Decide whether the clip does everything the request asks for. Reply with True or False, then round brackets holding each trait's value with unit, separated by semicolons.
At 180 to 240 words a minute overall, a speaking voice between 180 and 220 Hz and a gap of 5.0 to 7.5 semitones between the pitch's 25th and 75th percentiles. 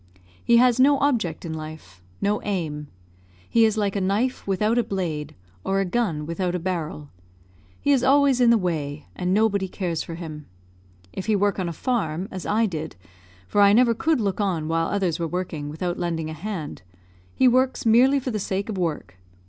True (195 wpm; 190 Hz; 5.5 semitones)